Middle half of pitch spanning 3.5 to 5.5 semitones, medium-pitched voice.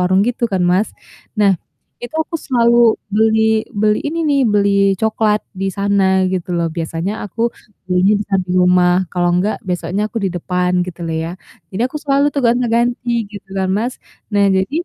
No: average, 4.3 semitones; high, 200 Hz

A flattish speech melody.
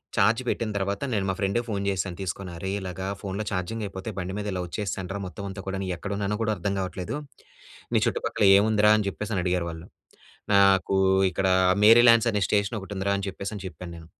Yes: narrow, 1.9 semitones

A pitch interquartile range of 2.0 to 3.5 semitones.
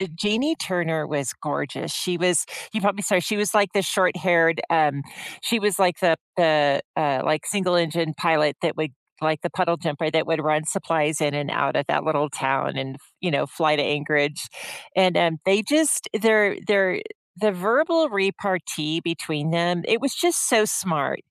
No: average, 4.3 semitones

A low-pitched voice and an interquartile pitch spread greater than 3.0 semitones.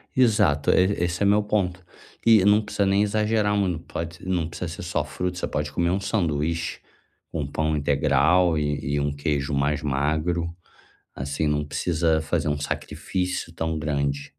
Yes: very low, 85 Hz; average, 4.1 semitones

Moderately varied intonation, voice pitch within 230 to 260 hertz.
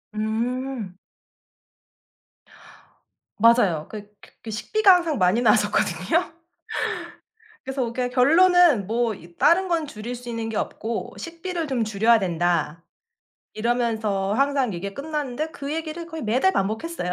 No: wide, 6.4 semitones; high, 235 Hz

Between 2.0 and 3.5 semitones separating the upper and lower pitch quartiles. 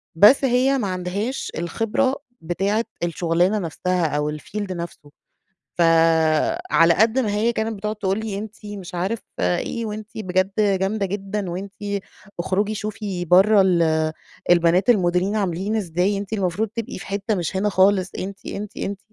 Yes: average, 3.2 semitones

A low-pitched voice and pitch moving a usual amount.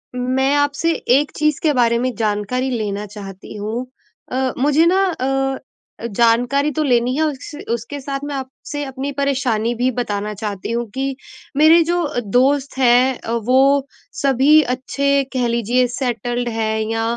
No: very high, 255 Hz; average, 3.2 semitones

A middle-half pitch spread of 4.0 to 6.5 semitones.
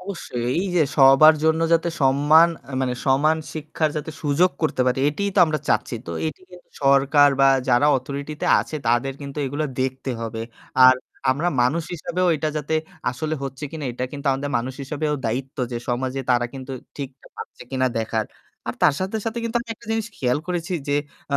No: average, 3.4 semitones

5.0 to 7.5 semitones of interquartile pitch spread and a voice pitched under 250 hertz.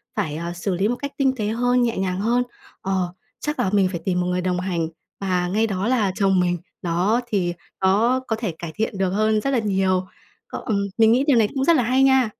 No: average, 4.6 semitones; high, 200 Hz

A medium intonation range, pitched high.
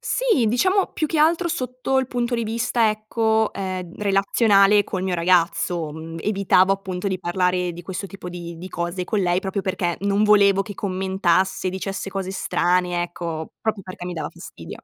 Yes: average, 3.1 semitones; high, 195 Hz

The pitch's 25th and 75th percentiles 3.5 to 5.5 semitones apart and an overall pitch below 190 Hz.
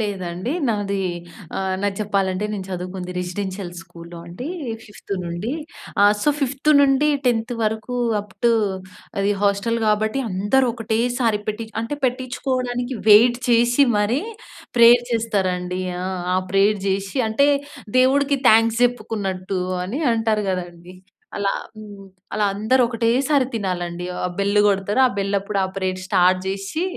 No: average, 4.1 semitones; high, 210 Hz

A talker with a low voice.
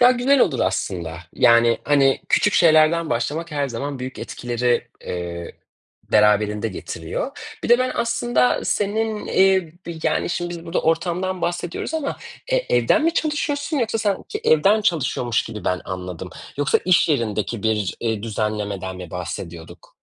No: medium, 145 Hz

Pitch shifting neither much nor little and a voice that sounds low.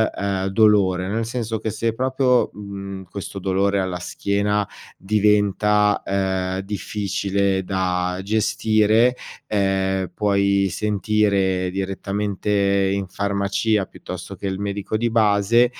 No: narrow, 1.8 semitones; low, 100 Hz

